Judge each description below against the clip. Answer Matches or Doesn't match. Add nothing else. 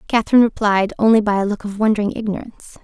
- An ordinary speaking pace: Matches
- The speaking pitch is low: Doesn't match